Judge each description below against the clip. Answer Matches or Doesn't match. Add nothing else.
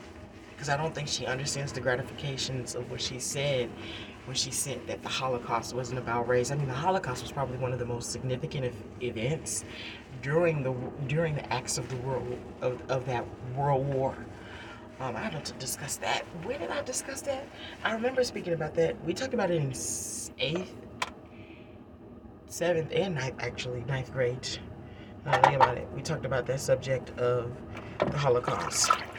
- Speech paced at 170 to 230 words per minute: Matches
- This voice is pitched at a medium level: Doesn't match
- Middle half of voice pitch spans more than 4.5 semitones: Doesn't match